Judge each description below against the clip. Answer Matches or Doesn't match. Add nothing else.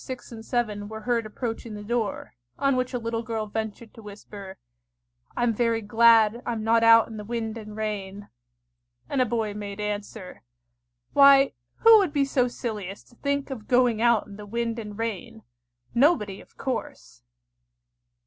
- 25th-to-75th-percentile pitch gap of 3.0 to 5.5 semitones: Doesn't match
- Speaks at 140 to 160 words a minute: Doesn't match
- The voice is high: Matches